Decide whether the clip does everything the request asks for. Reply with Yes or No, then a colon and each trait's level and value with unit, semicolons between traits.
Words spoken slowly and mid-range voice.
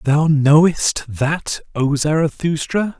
Yes: slow, 100 wpm; medium, 150 Hz